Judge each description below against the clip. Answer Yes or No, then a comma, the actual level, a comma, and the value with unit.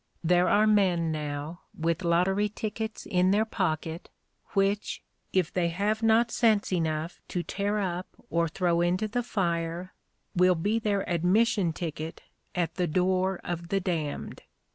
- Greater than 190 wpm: No, average, 145 wpm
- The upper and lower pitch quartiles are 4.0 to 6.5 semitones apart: No, average, 3.2 semitones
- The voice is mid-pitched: Yes, medium, 180 Hz